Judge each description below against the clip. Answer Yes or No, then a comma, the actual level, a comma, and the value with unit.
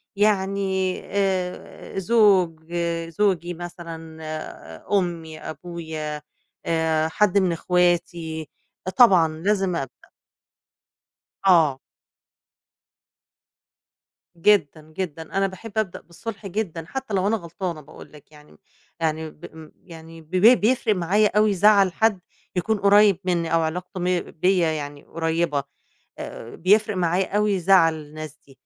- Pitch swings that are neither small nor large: Yes, average, 3.5 semitones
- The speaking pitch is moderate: Yes, medium, 175 Hz